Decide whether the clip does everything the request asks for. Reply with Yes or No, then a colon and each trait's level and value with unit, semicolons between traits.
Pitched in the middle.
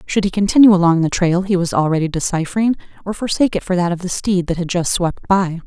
Yes: medium, 180 Hz